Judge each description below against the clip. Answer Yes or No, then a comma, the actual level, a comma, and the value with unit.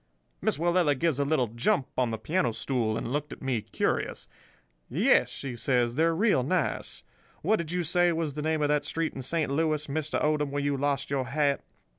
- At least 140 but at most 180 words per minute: No, fast, 205 wpm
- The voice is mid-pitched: Yes, medium, 145 Hz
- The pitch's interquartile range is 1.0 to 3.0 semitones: No, average, 3.4 semitones